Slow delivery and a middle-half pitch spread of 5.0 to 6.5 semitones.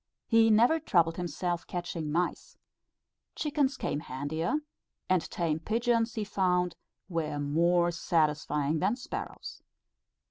Yes: slow, 110 wpm; average, 5.3 semitones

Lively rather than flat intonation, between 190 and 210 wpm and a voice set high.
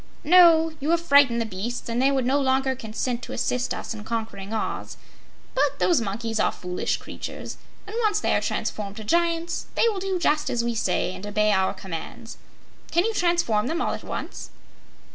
Yes: wide, 7.6 semitones; average, 195 wpm; high, 245 Hz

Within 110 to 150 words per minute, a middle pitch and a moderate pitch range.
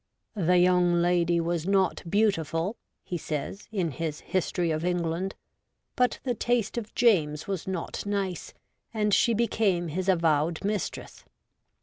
Yes: average, 145 wpm; medium, 180 Hz; average, 3.3 semitones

